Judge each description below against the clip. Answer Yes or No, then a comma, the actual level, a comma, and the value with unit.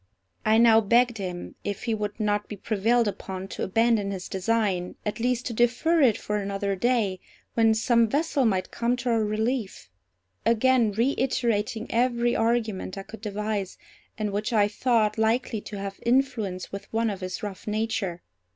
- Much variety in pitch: No, average, 2.8 semitones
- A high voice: Yes, high, 220 Hz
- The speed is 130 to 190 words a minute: Yes, average, 170 wpm